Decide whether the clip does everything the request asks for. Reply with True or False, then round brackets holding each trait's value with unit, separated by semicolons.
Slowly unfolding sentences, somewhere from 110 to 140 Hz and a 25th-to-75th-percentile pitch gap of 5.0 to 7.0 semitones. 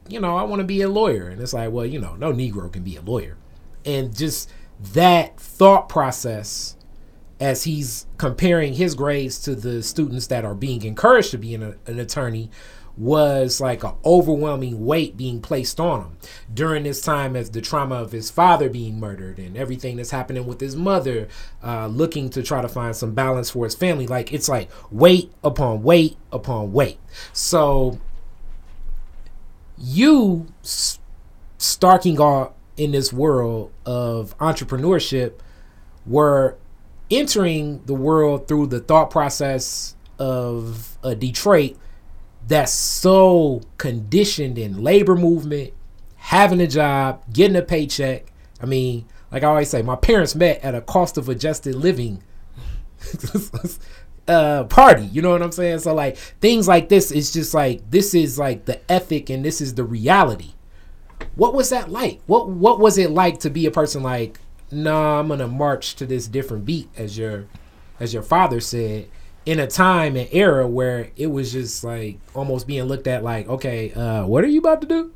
False (170 wpm; 135 Hz; 5.3 semitones)